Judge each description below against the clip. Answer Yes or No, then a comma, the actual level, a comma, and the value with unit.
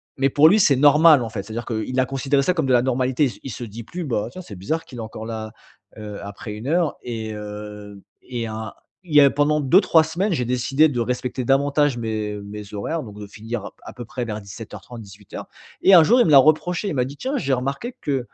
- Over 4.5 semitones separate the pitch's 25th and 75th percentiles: Yes, average, 5.2 semitones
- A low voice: Yes, low, 125 Hz